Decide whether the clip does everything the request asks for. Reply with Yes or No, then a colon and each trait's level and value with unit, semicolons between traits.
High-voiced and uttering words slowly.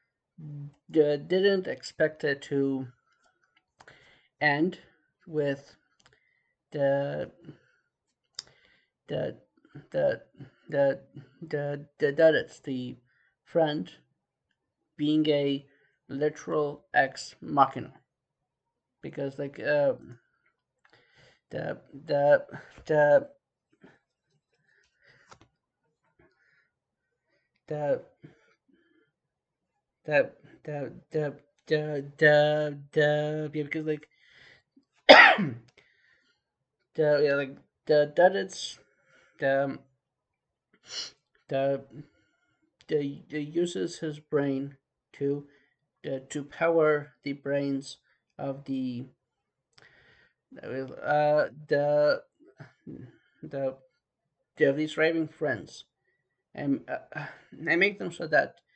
No: medium, 150 Hz; slow, 75 wpm